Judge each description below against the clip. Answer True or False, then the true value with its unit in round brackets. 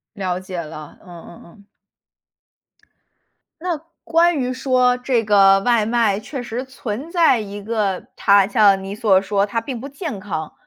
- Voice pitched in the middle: False (215 Hz)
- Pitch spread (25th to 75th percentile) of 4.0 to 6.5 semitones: True (4.5 semitones)